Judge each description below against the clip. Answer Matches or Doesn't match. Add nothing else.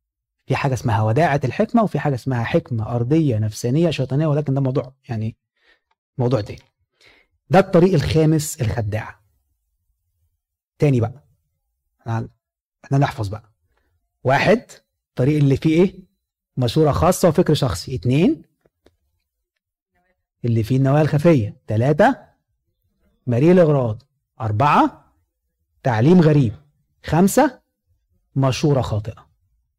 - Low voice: Matches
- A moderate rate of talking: Matches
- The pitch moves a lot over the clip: Matches